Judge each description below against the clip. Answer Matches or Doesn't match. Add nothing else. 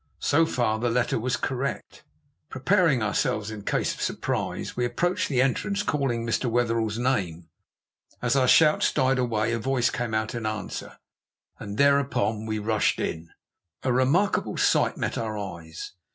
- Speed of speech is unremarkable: Matches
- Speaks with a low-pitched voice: Matches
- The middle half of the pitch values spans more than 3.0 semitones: Matches